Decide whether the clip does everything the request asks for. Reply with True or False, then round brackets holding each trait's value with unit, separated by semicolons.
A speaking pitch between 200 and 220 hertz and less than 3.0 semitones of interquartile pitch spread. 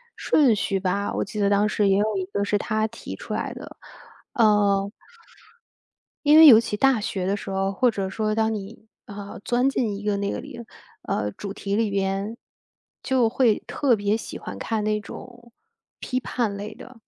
True (210 Hz; 2.4 semitones)